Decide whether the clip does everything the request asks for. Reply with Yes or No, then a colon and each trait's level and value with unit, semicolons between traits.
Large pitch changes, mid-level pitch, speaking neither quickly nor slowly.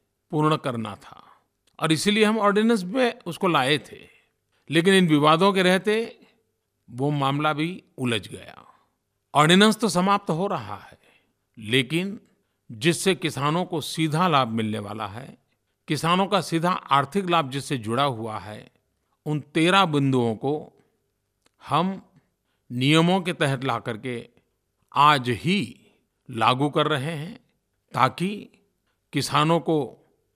Yes: wide, 6.1 semitones; medium, 155 Hz; average, 125 wpm